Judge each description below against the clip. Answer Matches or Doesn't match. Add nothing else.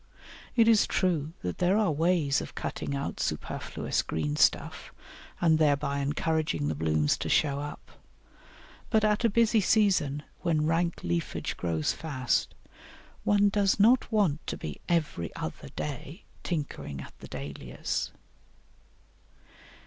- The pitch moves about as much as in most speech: Doesn't match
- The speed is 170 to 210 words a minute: Doesn't match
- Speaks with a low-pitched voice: Doesn't match